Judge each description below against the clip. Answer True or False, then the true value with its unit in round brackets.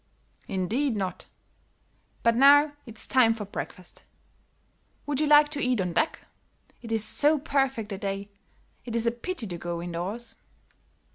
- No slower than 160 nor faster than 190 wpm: False (150 wpm)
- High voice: True (230 Hz)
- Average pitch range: False (6.1 semitones)